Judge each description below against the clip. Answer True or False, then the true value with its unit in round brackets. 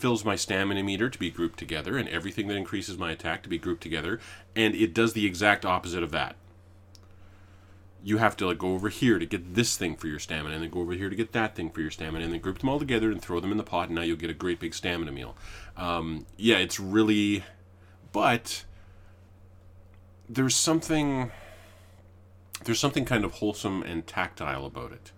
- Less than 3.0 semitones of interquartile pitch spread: False (3.3 semitones)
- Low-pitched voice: True (95 Hz)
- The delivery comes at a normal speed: False (210 wpm)